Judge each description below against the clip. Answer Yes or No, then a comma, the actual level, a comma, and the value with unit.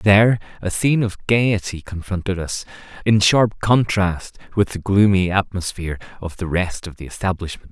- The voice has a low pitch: Yes, very low, 95 Hz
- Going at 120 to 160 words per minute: Yes, average, 155 wpm